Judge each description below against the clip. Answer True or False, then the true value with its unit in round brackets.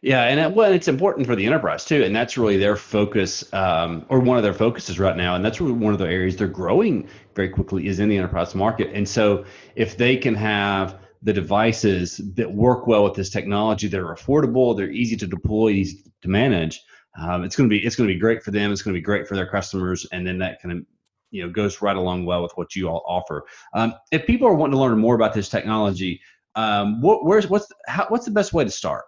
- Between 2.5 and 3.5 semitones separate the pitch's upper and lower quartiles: True (3.1 semitones)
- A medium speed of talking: False (250 wpm)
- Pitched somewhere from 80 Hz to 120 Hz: True (105 Hz)